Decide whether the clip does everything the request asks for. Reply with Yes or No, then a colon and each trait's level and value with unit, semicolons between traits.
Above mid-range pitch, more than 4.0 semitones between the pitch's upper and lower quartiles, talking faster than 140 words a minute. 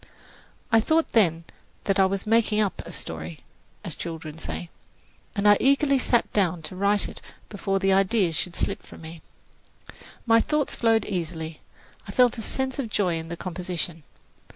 Yes: high, 195 Hz; average, 5.2 semitones; average, 170 wpm